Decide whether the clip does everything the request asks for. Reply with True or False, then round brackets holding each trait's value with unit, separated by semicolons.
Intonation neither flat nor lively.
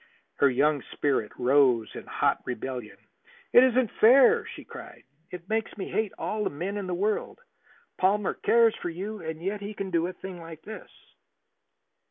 False (6.4 semitones)